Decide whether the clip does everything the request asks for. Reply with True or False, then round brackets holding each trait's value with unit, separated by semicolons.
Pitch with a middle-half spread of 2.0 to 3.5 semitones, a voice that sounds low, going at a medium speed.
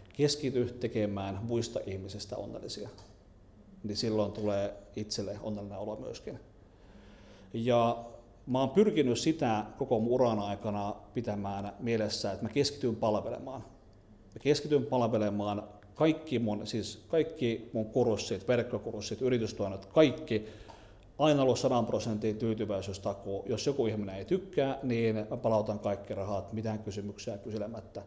True (3.0 semitones; 110 Hz; 120 wpm)